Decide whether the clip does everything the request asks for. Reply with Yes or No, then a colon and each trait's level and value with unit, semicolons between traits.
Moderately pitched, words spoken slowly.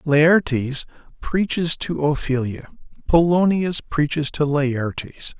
Yes: medium, 150 Hz; slow, 90 wpm